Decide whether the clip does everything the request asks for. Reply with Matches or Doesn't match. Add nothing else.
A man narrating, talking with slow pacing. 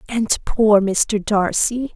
Doesn't match